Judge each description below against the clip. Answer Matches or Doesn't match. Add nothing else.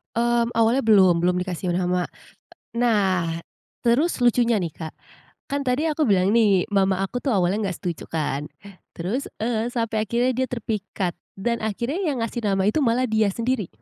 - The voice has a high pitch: Matches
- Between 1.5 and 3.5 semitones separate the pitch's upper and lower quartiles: Doesn't match